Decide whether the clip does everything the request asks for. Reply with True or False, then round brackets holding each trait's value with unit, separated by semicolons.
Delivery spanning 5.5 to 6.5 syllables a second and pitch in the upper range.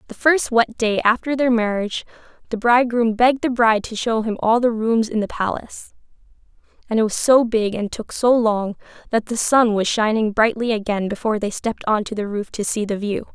True (5.6 syllables/s; 225 Hz)